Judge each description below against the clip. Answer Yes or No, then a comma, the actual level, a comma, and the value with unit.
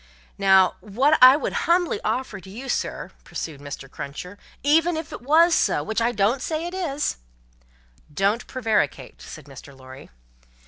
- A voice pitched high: Yes, high, 215 Hz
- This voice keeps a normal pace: Yes, average, 165 wpm